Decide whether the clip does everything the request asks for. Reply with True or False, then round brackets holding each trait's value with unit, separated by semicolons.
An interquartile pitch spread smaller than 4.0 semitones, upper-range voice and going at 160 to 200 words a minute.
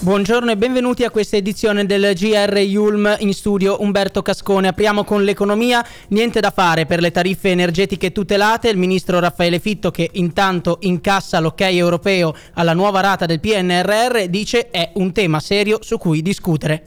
True (2.8 semitones; 195 Hz; 165 wpm)